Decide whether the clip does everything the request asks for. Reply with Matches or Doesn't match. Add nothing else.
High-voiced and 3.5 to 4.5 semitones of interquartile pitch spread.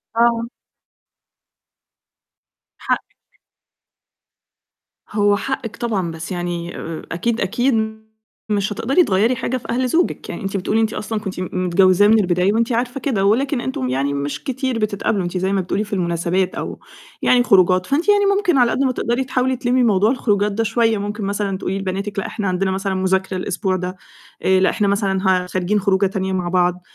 Matches